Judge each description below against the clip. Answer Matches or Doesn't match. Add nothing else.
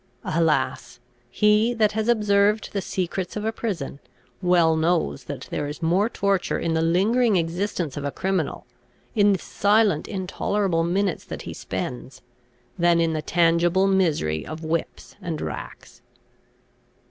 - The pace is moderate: Matches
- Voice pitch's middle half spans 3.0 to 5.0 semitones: Matches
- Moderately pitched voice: Matches